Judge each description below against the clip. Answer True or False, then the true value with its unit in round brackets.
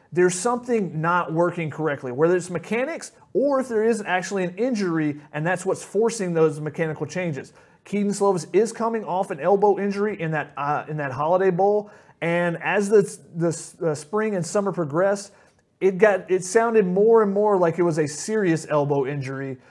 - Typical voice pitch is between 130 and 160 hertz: False (180 Hz)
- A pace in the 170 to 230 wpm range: True (185 wpm)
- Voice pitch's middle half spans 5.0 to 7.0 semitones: False (4.4 semitones)